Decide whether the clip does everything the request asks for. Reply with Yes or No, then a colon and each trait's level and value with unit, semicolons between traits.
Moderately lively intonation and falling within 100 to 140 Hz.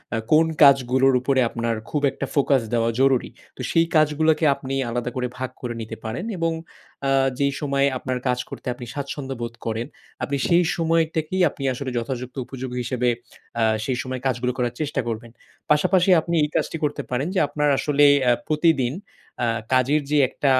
Yes: average, 3.2 semitones; low, 135 Hz